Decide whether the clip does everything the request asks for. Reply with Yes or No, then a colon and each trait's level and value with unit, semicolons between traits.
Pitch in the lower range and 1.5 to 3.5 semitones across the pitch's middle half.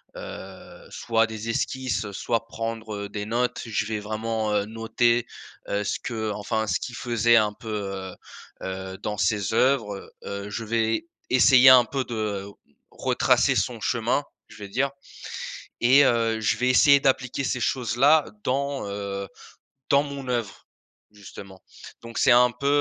Yes: low, 115 Hz; average, 3.2 semitones